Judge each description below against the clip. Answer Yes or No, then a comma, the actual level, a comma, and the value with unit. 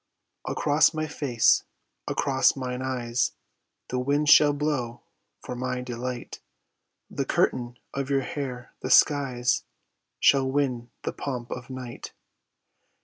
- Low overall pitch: Yes, low, 130 Hz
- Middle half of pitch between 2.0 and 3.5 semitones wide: Yes, narrow, 2.4 semitones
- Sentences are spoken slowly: Yes, slow, 120 wpm